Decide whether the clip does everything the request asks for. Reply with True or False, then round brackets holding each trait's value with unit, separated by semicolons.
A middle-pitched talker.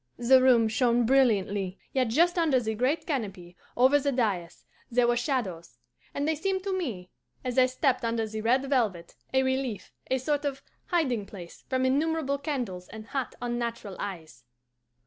False (250 Hz)